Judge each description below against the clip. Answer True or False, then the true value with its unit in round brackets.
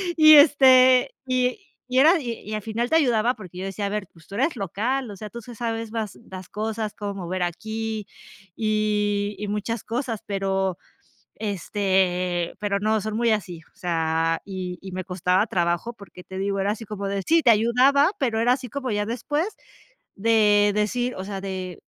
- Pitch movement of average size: True (3.6 semitones)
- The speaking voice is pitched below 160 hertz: False (210 Hz)